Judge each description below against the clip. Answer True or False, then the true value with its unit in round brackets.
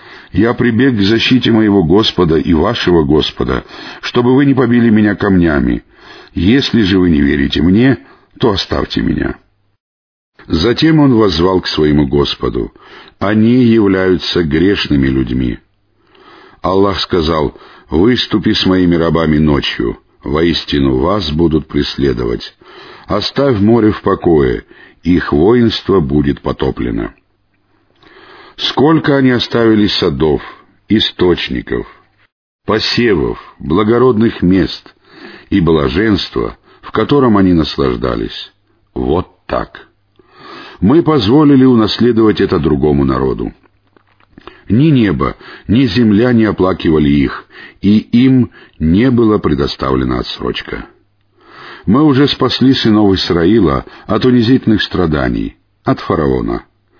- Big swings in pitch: True (6.7 semitones)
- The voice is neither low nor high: False (100 Hz)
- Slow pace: True (105 wpm)